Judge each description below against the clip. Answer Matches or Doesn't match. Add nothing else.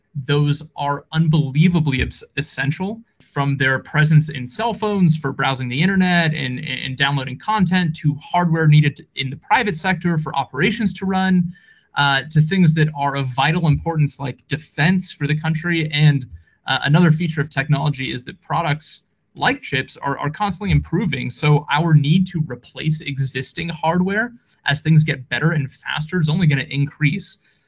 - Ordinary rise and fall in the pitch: Matches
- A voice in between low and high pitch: Matches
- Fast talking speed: Doesn't match